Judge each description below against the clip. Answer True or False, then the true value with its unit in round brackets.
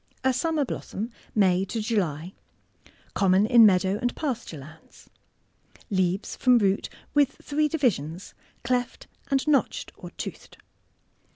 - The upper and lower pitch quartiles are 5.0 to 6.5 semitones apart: True (5.6 semitones)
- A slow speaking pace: True (120 wpm)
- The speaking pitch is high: True (215 Hz)